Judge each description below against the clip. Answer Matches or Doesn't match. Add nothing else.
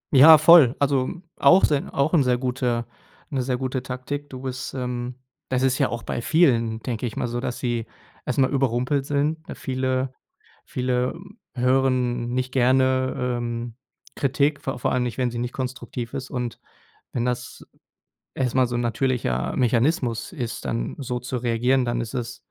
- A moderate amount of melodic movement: Doesn't match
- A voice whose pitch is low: Matches